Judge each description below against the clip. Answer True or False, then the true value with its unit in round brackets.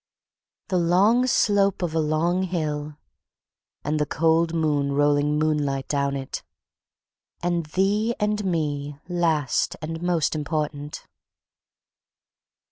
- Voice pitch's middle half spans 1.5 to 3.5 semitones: True (3.2 semitones)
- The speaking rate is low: True (110 wpm)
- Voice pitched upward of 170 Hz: False (160 Hz)